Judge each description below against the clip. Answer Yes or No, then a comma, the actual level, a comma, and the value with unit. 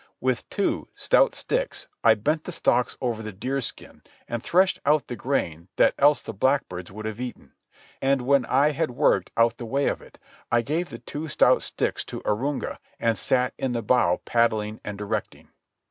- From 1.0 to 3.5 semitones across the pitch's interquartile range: No, average, 4.4 semitones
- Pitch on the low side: Yes, low, 125 Hz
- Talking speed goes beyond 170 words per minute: Yes, average, 185 wpm